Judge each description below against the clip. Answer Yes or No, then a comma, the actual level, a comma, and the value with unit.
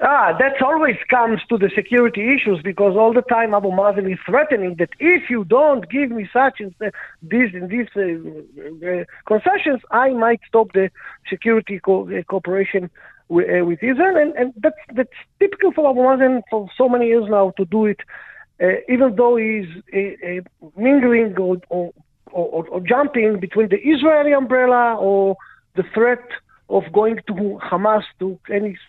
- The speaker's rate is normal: Yes, average, 175 wpm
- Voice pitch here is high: Yes, high, 220 Hz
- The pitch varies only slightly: No, average, 4.8 semitones